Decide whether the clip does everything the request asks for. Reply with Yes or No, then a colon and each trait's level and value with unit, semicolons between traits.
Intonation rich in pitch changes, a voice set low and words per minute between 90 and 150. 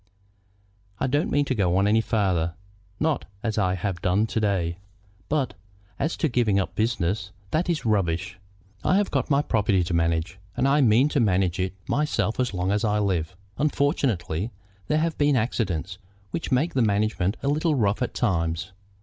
No: wide, 6.6 semitones; low, 105 Hz; average, 180 wpm